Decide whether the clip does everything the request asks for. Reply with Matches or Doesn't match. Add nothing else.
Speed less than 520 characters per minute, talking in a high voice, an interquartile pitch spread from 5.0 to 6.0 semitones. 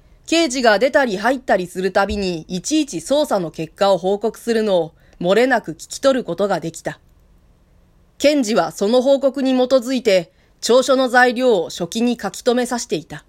Matches